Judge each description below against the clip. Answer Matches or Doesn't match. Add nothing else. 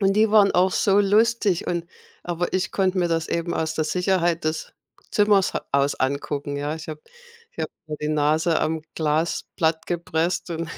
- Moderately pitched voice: Matches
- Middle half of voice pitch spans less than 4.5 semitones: Matches